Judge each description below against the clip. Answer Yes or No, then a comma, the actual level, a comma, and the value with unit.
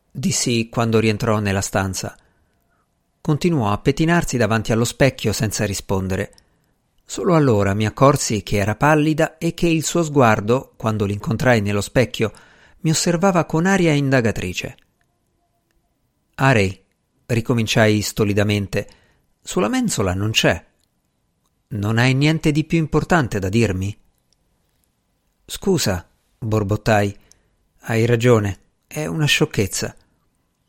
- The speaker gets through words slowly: Yes, slow, 110 wpm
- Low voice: Yes, low, 115 Hz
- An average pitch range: No, wide, 6.4 semitones